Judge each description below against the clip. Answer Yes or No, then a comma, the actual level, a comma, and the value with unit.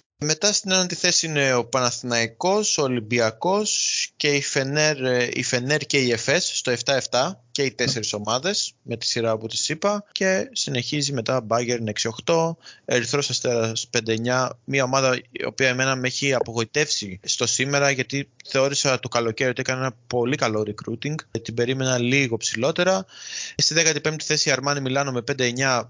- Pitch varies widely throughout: No, average, 3.4 semitones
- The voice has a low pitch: Yes, low, 130 Hz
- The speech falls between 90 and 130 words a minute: No, average, 160 wpm